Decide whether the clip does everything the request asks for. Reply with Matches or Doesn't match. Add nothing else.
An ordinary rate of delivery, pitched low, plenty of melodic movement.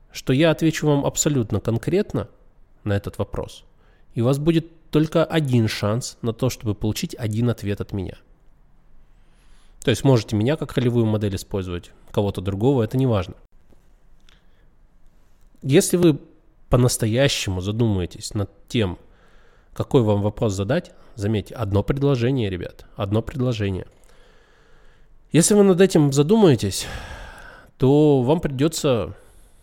Matches